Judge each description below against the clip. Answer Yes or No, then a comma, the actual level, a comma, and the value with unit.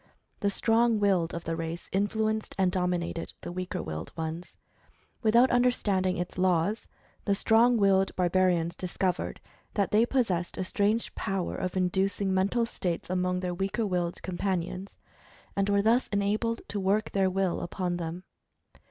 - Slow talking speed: No, average, 155 wpm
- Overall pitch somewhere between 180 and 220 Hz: Yes, high, 190 Hz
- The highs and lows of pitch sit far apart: No, narrow, 2.6 semitones